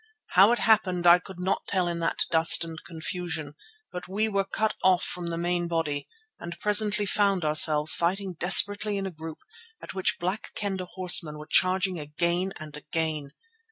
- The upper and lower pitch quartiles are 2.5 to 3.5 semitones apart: Yes, average, 2.9 semitones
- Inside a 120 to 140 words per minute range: No, average, 175 wpm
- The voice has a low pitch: No, medium, 180 Hz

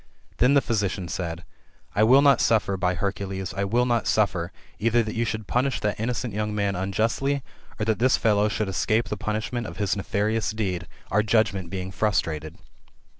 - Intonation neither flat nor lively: Yes, average, 3.0 semitones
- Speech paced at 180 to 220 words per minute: Yes, average, 185 wpm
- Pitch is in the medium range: No, low, 105 Hz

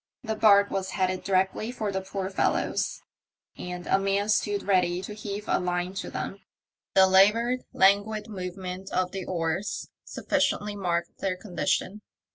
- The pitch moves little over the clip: Yes, narrow, 1.9 semitones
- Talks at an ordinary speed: Yes, average, 150 wpm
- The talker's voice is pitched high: Yes, high, 195 Hz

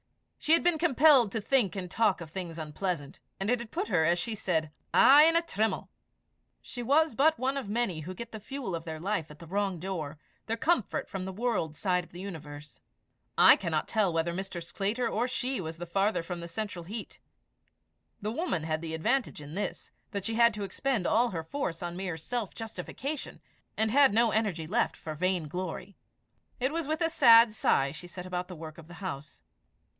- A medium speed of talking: No, fast, 215 wpm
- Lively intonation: Yes, wide, 5.9 semitones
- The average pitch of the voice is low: No, high, 195 Hz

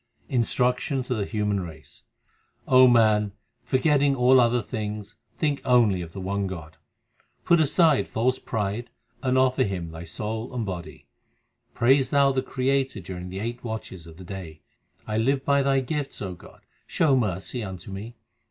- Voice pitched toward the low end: Yes, low, 115 Hz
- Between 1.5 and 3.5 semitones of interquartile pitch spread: No, average, 5.2 semitones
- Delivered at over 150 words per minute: Yes, average, 160 wpm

